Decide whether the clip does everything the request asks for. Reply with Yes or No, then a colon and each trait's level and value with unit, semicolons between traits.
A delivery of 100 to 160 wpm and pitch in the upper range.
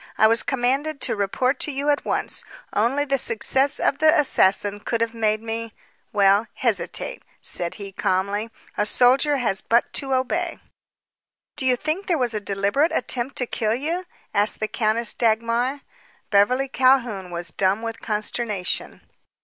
Yes: average, 155 wpm; high, 235 Hz